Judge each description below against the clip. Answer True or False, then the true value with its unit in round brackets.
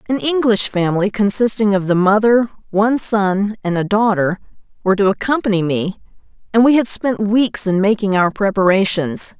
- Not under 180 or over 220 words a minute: False (160 wpm)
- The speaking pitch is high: True (205 Hz)